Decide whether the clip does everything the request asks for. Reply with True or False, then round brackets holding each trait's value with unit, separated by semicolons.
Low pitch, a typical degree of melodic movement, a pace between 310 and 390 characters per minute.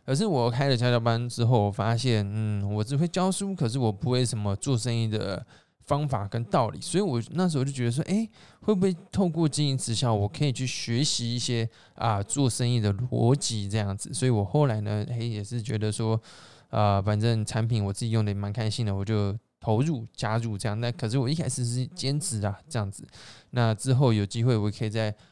True (120 Hz; 3.6 semitones; 320 characters per minute)